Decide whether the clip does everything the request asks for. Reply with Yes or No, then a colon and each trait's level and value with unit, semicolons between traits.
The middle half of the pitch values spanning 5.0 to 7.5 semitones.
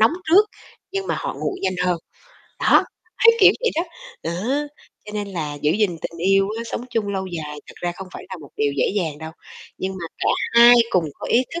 Yes: wide, 5.6 semitones